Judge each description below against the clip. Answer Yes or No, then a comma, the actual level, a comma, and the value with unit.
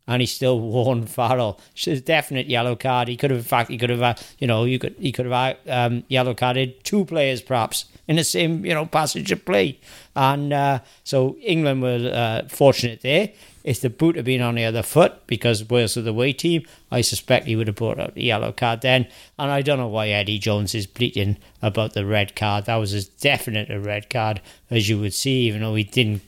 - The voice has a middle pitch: No, low, 125 Hz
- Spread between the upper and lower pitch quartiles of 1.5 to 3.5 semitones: Yes, average, 3.2 semitones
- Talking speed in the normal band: No, fast, 235 wpm